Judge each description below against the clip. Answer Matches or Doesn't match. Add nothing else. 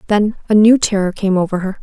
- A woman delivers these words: Matches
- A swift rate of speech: Matches